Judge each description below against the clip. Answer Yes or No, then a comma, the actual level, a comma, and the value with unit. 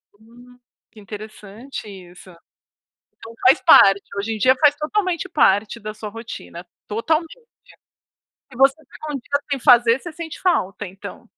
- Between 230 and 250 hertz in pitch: Yes, high, 235 Hz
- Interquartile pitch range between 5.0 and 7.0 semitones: Yes, wide, 5.4 semitones